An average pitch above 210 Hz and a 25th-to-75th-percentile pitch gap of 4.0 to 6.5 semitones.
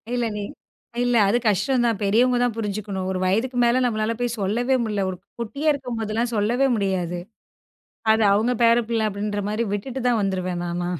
No: high, 220 Hz; average, 3.3 semitones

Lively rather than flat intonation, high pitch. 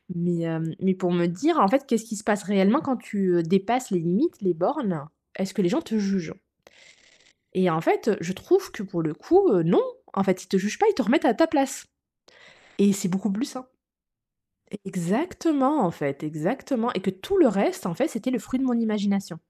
Yes: wide, 6.1 semitones; high, 200 Hz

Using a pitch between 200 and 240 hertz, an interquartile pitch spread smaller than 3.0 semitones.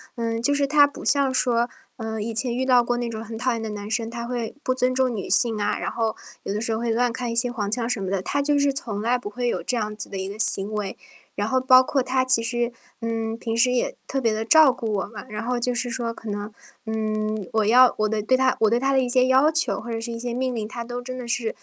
Yes: high, 235 Hz; narrow, 2.4 semitones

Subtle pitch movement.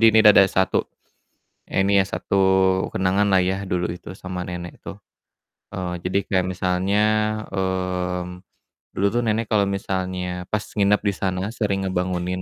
Yes: narrow, 1.4 semitones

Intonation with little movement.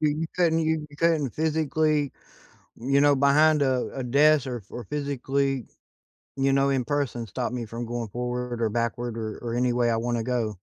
No: average, 3.4 semitones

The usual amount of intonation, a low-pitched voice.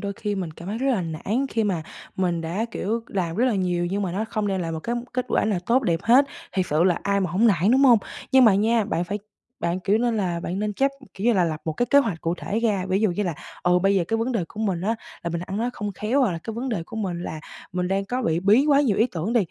No: average, 4.4 semitones; high, 200 Hz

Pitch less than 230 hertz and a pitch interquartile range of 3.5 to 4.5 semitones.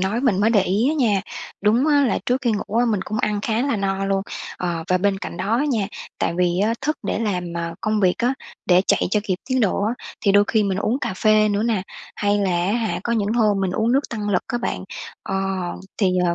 No: high, 210 Hz; average, 3.1 semitones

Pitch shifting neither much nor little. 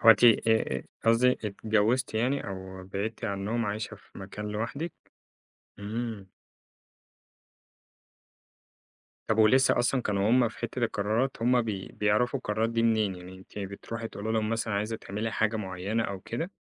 No: narrow, 2.3 semitones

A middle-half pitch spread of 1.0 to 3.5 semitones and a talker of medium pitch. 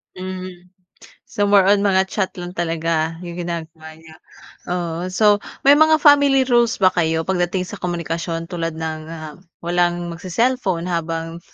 Yes: narrow, 2.5 semitones; medium, 175 Hz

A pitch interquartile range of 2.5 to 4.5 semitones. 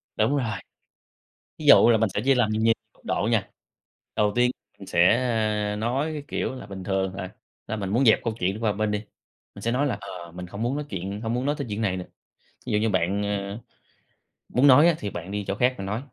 Yes: average, 3.8 semitones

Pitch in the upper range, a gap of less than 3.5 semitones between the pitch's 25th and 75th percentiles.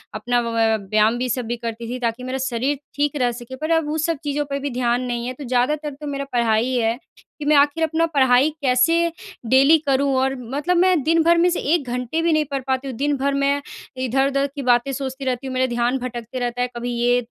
Yes: very high, 260 Hz; average, 3.1 semitones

